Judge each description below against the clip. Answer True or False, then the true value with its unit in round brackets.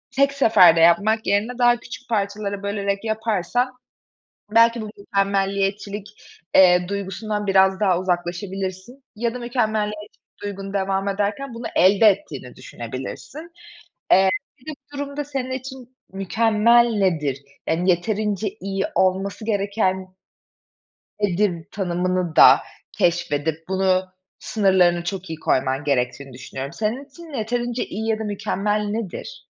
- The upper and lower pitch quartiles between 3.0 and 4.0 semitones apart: True (3.4 semitones)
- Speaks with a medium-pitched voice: False (200 Hz)